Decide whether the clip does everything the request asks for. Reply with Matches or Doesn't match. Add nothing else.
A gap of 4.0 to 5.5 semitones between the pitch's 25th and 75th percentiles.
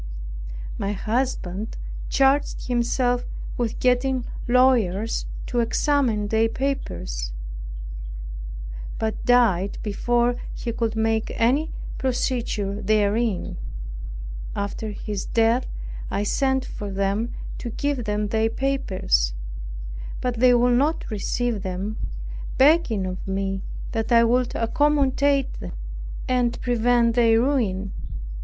Doesn't match